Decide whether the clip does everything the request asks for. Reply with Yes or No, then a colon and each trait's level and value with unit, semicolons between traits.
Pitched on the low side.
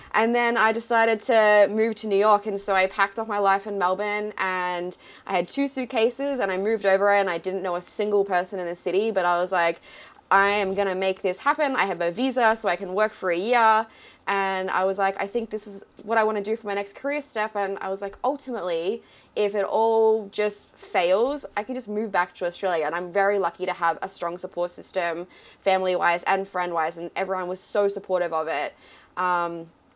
No: high, 200 Hz